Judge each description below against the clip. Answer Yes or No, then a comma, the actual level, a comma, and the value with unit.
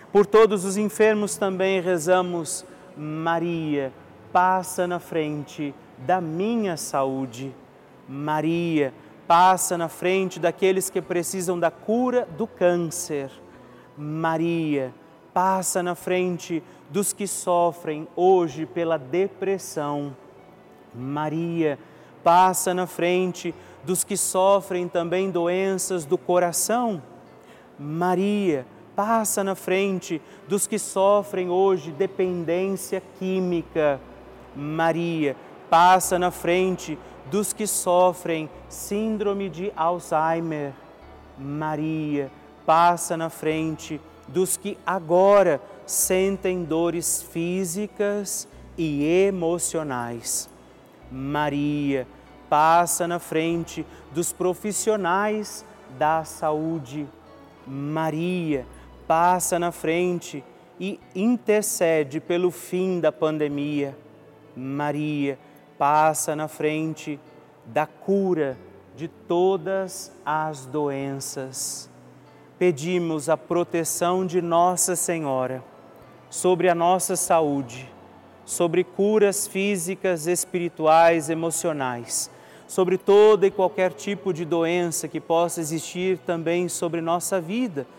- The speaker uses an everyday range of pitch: Yes, average, 3.4 semitones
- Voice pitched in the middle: Yes, medium, 170 Hz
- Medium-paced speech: No, slow, 90 wpm